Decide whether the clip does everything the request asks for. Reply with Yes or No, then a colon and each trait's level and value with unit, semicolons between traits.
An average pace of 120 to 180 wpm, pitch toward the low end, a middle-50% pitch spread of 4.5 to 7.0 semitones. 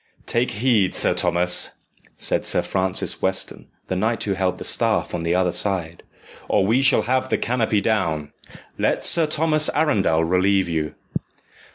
Yes: average, 160 wpm; very low, 95 Hz; average, 5.0 semitones